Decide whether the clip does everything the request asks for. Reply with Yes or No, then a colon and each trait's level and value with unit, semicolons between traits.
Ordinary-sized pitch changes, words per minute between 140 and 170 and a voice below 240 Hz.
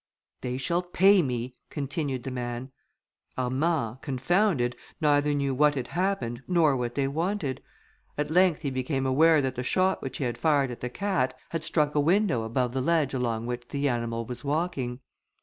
No: average, 4.5 semitones; average, 180 wpm; low, 135 Hz